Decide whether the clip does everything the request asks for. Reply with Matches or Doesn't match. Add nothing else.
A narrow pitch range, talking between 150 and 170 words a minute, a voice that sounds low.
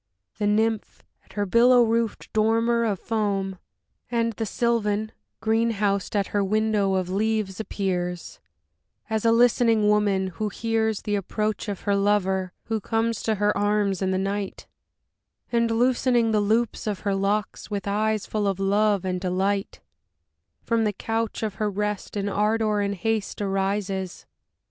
Doesn't match